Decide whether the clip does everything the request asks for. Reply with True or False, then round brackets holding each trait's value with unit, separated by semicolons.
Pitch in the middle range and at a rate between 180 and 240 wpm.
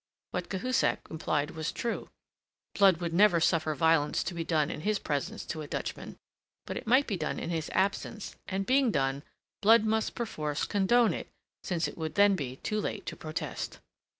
True (175 Hz; 185 wpm)